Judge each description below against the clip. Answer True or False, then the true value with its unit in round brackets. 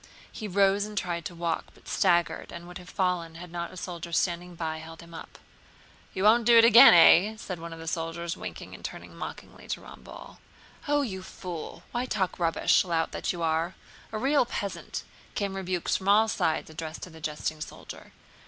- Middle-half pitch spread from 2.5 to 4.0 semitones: True (3.2 semitones)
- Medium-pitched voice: True (175 Hz)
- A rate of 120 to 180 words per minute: False (195 wpm)